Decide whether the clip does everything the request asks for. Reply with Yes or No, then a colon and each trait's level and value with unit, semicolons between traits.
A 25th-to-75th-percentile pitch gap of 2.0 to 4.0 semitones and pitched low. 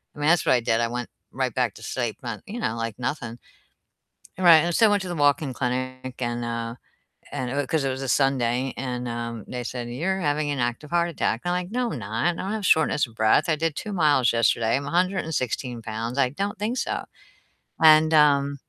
No: average, 5.0 semitones; low, 130 Hz